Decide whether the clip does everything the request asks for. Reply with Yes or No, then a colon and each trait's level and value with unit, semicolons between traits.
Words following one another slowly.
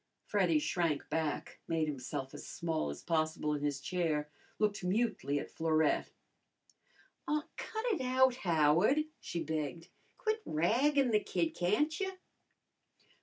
Yes: slow, 130 wpm